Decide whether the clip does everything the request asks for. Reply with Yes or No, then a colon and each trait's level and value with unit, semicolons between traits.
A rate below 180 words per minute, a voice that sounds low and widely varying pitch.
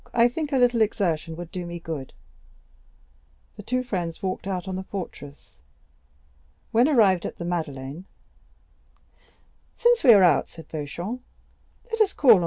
No: average, 165 wpm; medium, 185 Hz; wide, 6.4 semitones